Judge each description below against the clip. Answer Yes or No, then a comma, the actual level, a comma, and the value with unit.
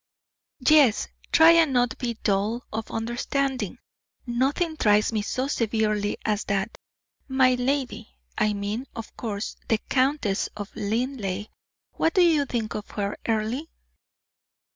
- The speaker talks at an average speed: No, slow, 130 wpm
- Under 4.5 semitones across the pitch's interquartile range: Yes, average, 4.1 semitones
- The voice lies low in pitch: No, high, 235 Hz